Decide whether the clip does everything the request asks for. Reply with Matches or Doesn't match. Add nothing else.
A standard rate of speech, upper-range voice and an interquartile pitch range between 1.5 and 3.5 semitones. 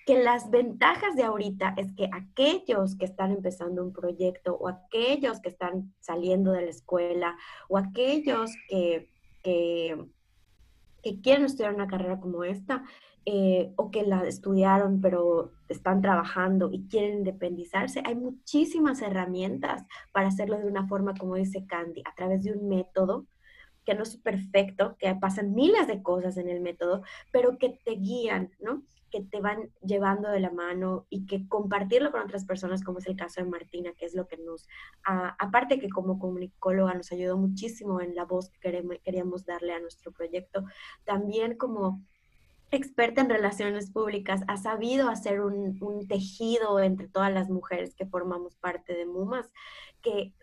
Matches